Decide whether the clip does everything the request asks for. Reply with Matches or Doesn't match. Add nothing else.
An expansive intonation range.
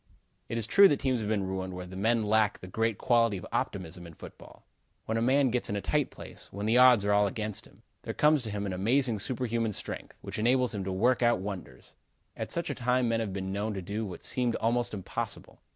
Doesn't match